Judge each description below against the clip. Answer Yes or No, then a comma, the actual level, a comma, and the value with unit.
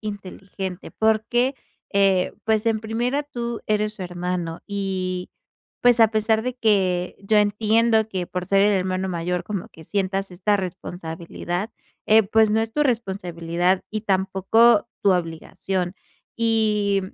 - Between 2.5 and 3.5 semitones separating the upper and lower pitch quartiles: Yes, average, 3.2 semitones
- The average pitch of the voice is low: No, high, 200 Hz